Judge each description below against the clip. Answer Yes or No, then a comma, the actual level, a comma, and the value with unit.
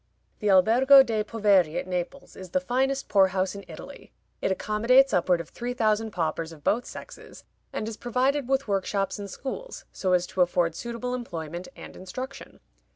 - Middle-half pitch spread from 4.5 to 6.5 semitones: Yes, average, 5.3 semitones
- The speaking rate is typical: Yes, average, 175 wpm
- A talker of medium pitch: No, high, 210 Hz